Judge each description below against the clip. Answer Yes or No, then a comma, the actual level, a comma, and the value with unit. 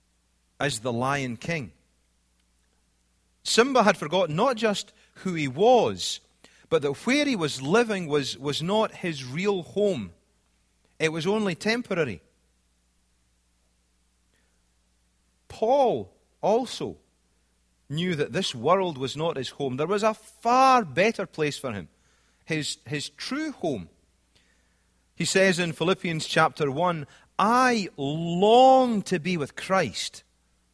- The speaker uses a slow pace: Yes, slow, 120 wpm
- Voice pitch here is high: No, medium, 150 Hz